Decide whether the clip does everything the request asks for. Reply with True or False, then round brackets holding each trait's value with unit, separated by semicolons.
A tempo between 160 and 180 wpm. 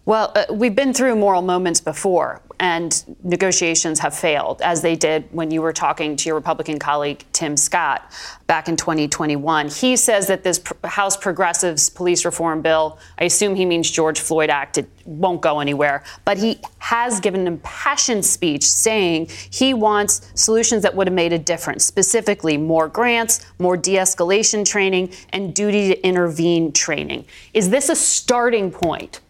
True (170 wpm)